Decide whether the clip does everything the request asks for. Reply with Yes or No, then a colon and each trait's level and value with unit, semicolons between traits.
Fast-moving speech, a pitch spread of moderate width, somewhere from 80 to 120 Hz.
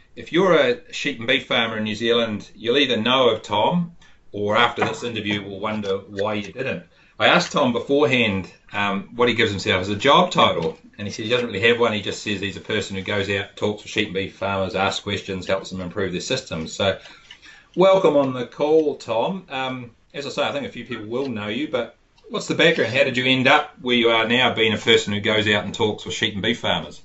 Yes: fast, 245 wpm; average, 3.8 semitones; low, 110 Hz